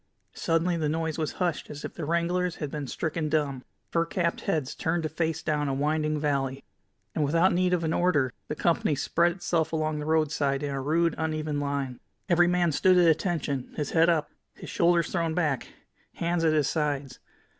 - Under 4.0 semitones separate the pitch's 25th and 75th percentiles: Yes, narrow, 2.5 semitones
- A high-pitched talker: No, medium, 160 Hz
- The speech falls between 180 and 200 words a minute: Yes, average, 195 wpm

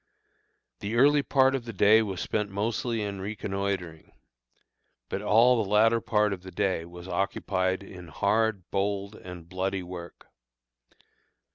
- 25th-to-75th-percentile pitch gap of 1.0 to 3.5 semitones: Yes, average, 2.9 semitones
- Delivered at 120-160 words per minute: Yes, average, 140 wpm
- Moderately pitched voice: No, low, 100 Hz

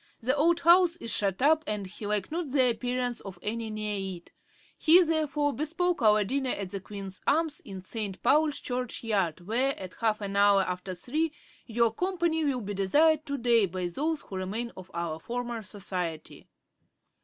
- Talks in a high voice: Yes, high, 230 Hz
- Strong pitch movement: Yes, wide, 6.9 semitones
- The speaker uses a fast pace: No, average, 180 wpm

